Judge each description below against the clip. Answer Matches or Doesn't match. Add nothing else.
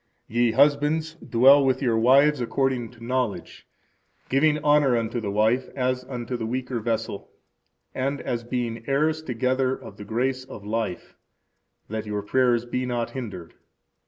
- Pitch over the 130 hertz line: Doesn't match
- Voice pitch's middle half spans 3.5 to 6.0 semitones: Doesn't match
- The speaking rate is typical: Matches